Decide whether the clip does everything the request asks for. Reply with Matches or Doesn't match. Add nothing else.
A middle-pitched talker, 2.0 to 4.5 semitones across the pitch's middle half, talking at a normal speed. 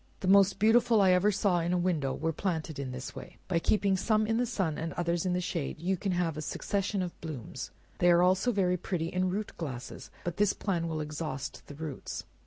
Doesn't match